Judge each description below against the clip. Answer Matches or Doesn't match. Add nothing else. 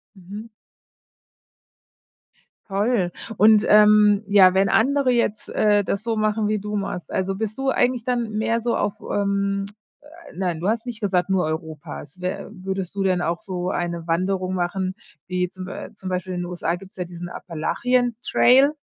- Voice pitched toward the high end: Matches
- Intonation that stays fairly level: Doesn't match